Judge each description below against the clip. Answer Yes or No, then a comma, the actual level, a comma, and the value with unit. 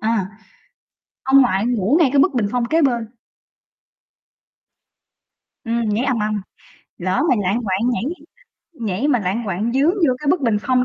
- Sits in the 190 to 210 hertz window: No, high, 235 Hz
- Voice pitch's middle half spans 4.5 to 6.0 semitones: No, average, 4.0 semitones